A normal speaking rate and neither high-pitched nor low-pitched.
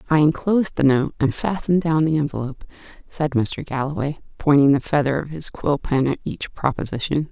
Yes: average, 180 wpm; medium, 145 Hz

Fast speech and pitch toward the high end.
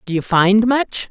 Yes: fast, 215 wpm; high, 215 Hz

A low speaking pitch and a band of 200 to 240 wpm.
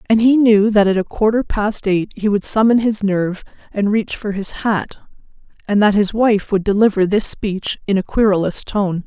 No: high, 205 Hz; fast, 205 wpm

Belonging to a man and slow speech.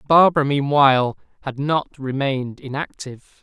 Yes: male; slow, 105 wpm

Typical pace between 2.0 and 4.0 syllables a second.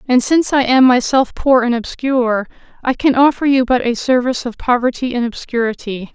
No: 5.5 syllables/s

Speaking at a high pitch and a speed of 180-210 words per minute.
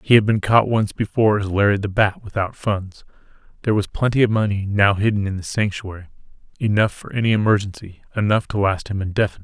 No: low, 105 Hz; average, 195 wpm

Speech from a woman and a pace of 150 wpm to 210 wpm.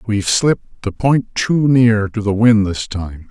No: male; average, 200 wpm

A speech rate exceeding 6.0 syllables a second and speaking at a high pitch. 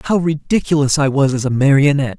No: 6.5 syllables/s; medium, 140 Hz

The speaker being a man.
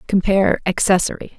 No: female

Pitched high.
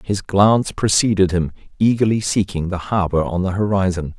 No: very low, 95 Hz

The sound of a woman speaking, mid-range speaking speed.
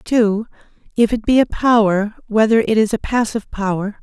Yes: female; average, 180 wpm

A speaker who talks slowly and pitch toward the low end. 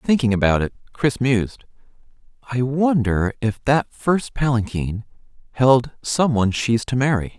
Yes: slow, 130 wpm; low, 125 Hz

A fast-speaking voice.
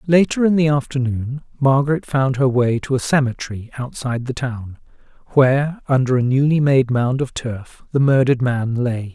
No: average, 170 wpm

